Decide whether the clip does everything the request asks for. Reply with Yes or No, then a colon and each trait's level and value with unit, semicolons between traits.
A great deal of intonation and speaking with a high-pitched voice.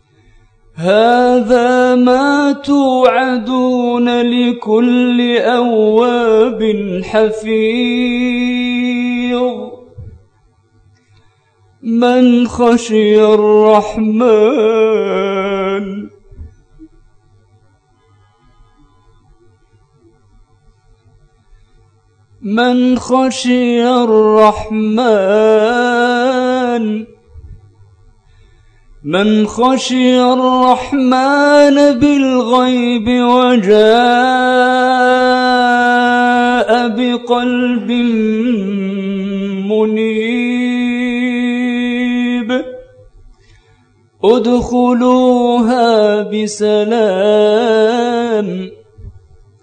Yes: wide, 8.9 semitones; high, 225 Hz